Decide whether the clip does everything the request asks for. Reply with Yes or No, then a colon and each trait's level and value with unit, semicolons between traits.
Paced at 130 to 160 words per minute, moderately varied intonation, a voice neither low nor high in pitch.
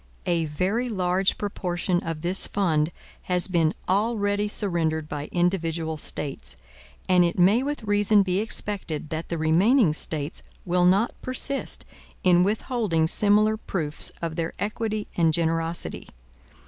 Yes: slow, 135 wpm; average, 4.0 semitones; medium, 180 Hz